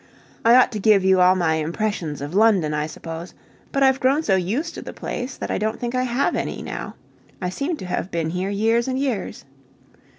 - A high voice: Yes, high, 205 Hz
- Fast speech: Yes, fast, 220 wpm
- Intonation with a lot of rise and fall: Yes, wide, 6.0 semitones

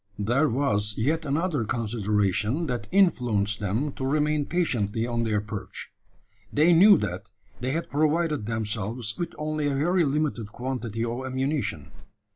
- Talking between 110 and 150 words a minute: Yes, average, 140 wpm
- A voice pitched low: Yes, low, 130 Hz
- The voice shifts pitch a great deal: Yes, wide, 5.7 semitones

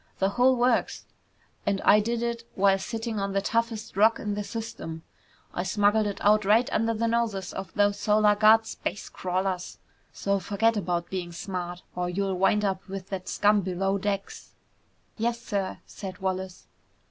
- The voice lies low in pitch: No, high, 200 Hz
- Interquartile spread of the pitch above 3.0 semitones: No, average, 2.7 semitones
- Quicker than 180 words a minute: No, average, 170 wpm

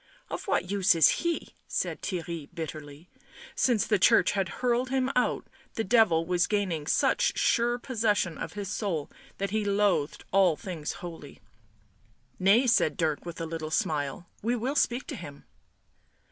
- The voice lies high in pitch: Yes, high, 195 Hz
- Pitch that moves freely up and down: Yes, wide, 5.9 semitones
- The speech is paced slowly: No, average, 160 wpm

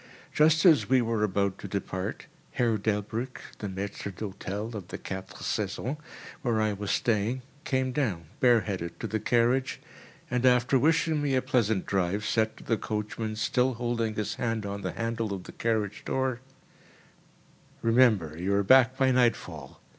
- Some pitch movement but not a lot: Yes, average, 3.8 semitones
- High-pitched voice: No, low, 110 Hz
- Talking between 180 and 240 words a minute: No, average, 160 wpm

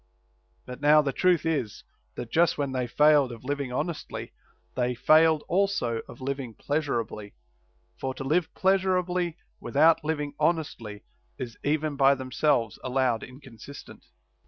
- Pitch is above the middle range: No, medium, 140 Hz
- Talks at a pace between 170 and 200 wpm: No, slow, 135 wpm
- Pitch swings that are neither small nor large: Yes, average, 4.1 semitones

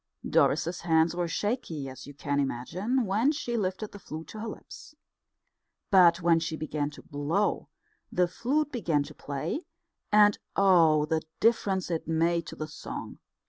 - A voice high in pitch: No, medium, 170 Hz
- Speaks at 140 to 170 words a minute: Yes, average, 160 wpm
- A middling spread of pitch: Yes, average, 5.0 semitones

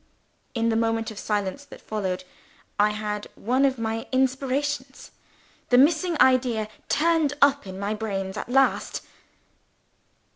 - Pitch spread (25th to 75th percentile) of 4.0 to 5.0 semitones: Yes, average, 4.4 semitones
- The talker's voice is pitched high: Yes, high, 230 Hz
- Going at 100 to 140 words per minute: Yes, slow, 135 wpm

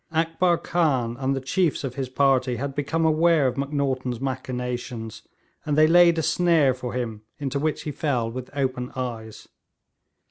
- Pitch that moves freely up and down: No, average, 3.8 semitones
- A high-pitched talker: No, low, 135 Hz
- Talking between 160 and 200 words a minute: Yes, average, 165 wpm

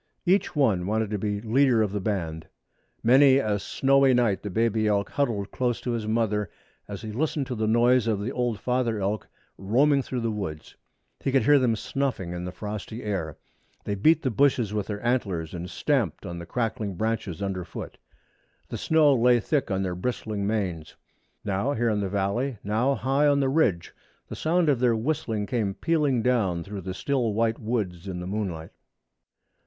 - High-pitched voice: No, low, 110 Hz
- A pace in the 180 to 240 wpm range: Yes, average, 190 wpm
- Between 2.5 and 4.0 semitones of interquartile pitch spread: No, average, 4.4 semitones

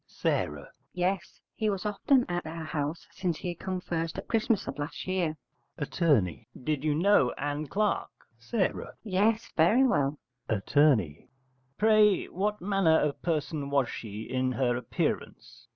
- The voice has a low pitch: No, medium, 170 Hz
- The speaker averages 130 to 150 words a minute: Yes, average, 145 wpm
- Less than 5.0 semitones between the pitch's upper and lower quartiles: No, wide, 5.6 semitones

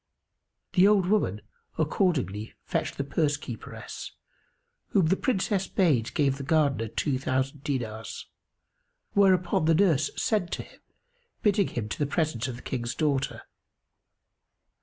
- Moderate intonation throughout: No, wide, 6.0 semitones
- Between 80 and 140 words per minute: Yes, slow, 135 wpm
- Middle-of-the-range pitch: Yes, medium, 150 Hz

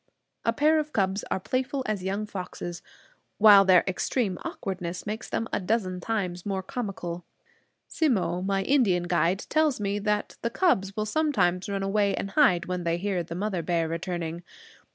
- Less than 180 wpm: Yes, average, 170 wpm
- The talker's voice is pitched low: No, high, 195 Hz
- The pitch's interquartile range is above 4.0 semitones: No, average, 3.3 semitones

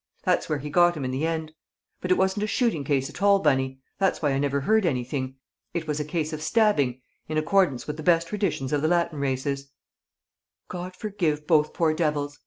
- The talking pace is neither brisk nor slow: No, fast, 210 wpm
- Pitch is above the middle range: No, medium, 155 Hz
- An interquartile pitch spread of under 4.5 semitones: Yes, average, 3.9 semitones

